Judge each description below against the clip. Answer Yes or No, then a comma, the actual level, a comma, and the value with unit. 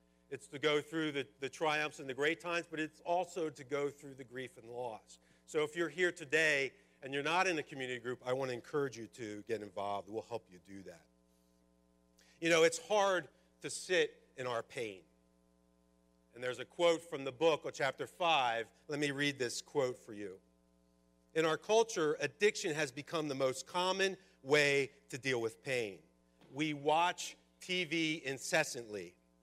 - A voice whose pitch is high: No, medium, 140 Hz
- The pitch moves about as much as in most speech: No, wide, 8.2 semitones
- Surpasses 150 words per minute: Yes, average, 185 wpm